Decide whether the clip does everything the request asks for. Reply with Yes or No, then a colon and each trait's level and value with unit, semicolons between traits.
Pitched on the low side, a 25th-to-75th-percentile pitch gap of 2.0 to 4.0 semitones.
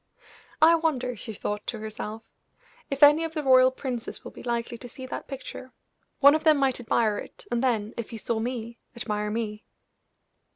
No: high, 245 Hz; average, 3.4 semitones